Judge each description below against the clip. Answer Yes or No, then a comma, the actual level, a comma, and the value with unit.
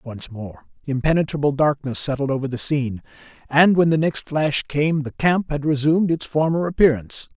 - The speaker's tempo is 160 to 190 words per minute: Yes, average, 170 wpm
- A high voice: No, medium, 145 Hz